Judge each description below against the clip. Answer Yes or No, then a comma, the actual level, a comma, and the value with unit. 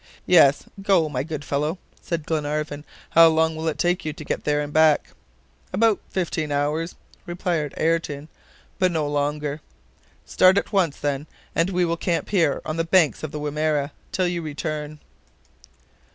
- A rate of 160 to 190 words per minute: Yes, average, 165 wpm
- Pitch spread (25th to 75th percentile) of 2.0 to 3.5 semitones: Yes, narrow, 2.5 semitones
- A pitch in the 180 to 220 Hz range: No, medium, 155 Hz